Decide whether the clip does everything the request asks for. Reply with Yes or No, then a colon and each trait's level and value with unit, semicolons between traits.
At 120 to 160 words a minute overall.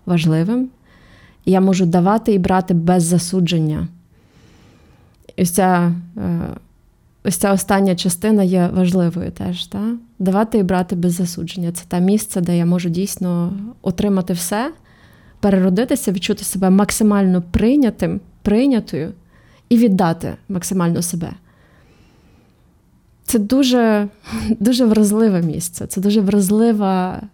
No: average, 110 wpm